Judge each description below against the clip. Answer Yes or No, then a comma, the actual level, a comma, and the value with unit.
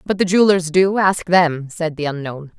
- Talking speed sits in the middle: No, fast, 210 wpm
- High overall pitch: No, medium, 170 Hz